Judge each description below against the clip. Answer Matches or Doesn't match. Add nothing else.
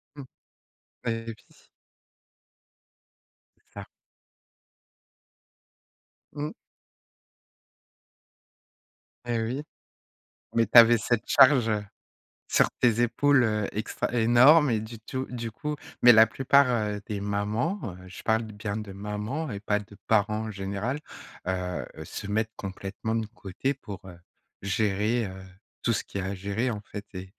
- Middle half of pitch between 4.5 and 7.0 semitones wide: Doesn't match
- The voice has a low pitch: Matches